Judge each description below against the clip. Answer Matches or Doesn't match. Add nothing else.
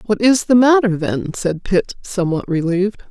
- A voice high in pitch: Matches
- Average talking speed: Matches